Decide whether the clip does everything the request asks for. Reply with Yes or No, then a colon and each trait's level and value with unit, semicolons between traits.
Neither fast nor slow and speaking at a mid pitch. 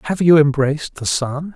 Yes: average, 195 wpm; medium, 150 Hz